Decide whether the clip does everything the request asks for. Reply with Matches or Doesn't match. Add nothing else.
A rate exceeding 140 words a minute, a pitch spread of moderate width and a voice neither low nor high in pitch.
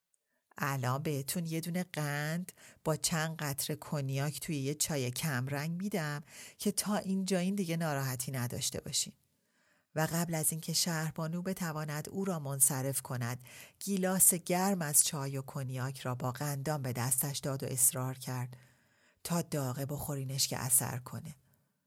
Matches